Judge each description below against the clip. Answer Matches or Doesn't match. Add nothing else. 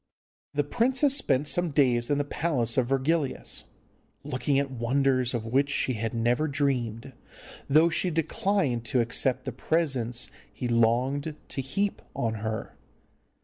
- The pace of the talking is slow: Doesn't match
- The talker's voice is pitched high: Doesn't match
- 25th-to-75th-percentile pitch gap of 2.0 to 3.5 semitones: Doesn't match